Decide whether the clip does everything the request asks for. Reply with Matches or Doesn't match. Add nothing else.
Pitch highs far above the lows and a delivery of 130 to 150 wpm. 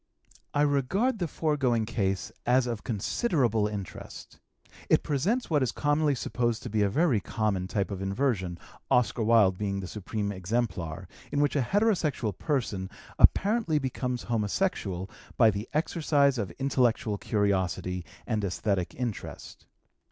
Matches